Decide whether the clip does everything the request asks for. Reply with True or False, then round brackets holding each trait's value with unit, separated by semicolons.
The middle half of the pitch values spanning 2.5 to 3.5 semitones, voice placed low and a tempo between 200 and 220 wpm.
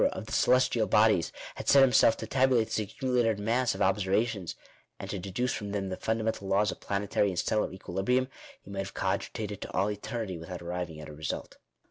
True (3.1 semitones; 105 Hz; 205 wpm)